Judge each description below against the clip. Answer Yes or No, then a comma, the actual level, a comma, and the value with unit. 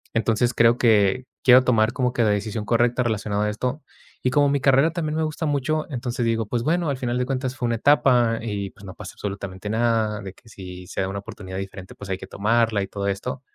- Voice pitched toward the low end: Yes, low, 115 Hz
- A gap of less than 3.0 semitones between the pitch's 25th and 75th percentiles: No, average, 3.8 semitones